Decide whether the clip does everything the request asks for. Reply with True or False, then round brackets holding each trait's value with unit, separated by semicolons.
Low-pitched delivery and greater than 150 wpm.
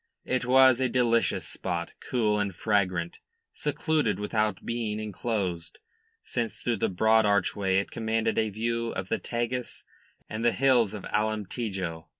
False (110 Hz; 145 wpm)